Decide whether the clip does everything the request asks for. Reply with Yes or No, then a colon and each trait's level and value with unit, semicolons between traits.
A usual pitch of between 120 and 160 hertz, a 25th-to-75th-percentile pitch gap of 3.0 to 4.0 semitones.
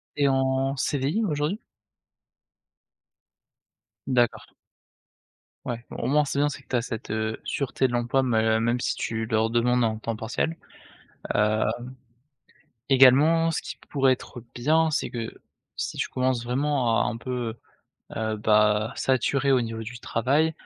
Yes: low, 125 Hz; average, 3.5 semitones